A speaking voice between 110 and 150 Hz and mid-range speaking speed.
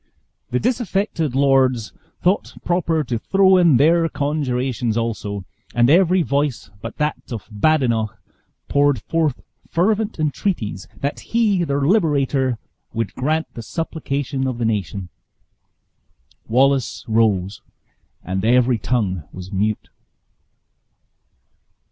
No: low, 135 Hz; slow, 110 wpm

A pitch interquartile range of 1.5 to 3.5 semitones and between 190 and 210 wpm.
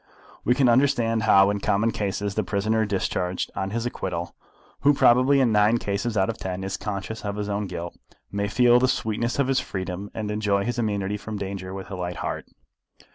Yes: average, 2.9 semitones; average, 200 wpm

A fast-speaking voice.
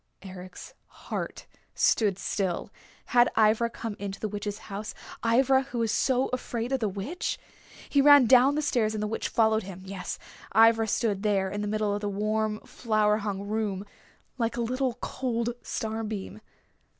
No: average, 170 wpm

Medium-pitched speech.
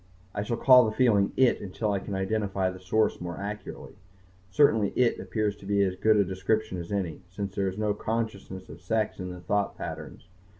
No: low, 100 Hz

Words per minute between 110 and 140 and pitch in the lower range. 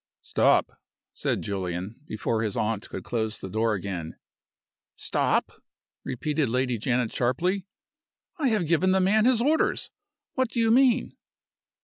Yes: slow, 135 wpm; low, 125 Hz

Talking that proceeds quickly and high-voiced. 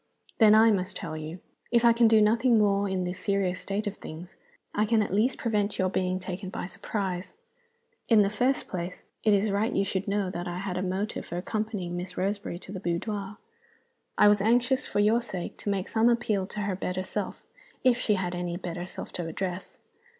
Yes: fast, 210 wpm; high, 200 Hz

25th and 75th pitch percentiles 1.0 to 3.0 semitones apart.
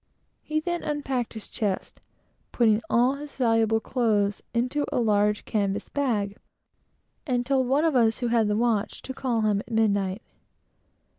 No: average, 3.8 semitones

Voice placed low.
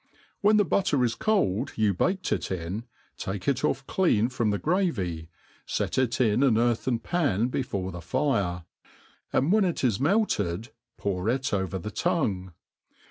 Yes: low, 115 Hz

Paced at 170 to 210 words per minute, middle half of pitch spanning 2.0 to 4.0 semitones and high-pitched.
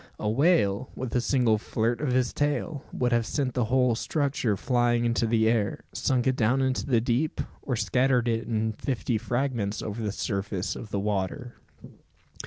No: average, 180 wpm; average, 2.9 semitones; low, 120 Hz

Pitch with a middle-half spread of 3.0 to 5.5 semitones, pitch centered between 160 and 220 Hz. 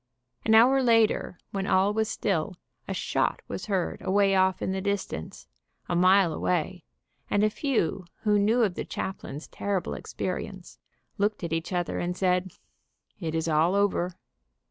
No: narrow, 2.6 semitones; high, 190 Hz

